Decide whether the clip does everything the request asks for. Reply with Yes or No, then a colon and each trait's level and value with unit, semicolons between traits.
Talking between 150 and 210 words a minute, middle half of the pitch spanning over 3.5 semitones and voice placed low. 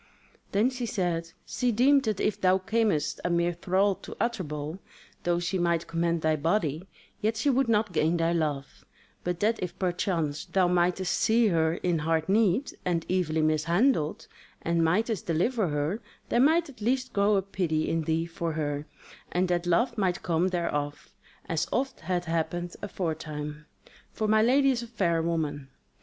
No: average, 170 wpm; average, 4.6 semitones; medium, 175 Hz